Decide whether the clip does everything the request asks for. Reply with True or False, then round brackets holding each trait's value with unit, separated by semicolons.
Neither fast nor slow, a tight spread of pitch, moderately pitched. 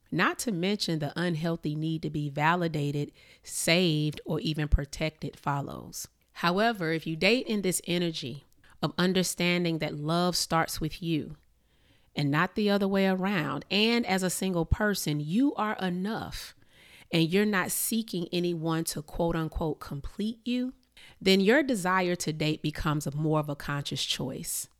False (155 wpm; 3.9 semitones; 170 Hz)